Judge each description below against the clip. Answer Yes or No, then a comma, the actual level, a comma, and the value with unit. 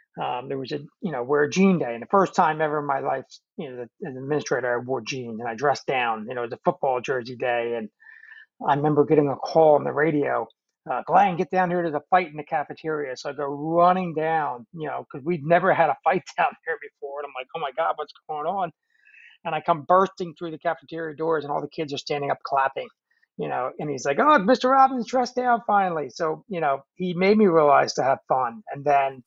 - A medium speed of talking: No, fast, 250 wpm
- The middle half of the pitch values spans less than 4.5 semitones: No, average, 4.8 semitones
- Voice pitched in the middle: Yes, medium, 160 Hz